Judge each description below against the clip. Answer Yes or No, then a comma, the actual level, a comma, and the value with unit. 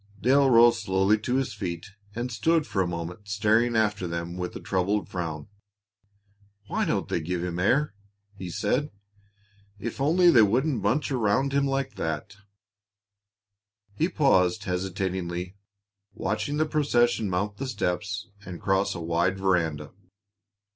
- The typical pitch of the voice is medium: No, low, 100 Hz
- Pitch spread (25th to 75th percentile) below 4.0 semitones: No, average, 5.1 semitones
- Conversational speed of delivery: Yes, average, 145 wpm